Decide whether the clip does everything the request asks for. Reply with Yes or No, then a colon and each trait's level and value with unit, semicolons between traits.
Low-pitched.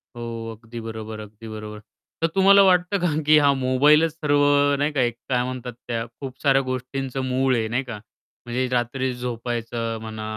Yes: low, 125 Hz